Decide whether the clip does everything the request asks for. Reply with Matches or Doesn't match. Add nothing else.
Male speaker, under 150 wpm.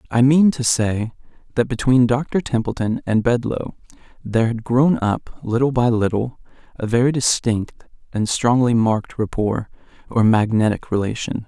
Matches